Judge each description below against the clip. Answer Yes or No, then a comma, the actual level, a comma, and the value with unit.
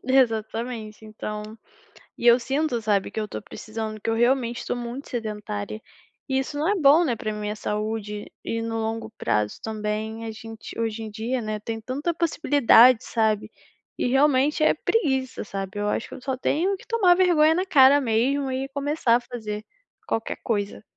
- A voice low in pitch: No, high, 230 Hz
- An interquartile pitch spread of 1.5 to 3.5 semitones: No, average, 4.0 semitones